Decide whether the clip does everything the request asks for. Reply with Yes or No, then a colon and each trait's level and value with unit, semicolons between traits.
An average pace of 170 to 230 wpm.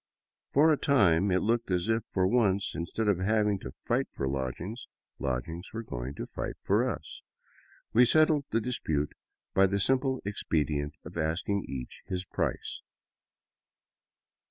No: average, 150 wpm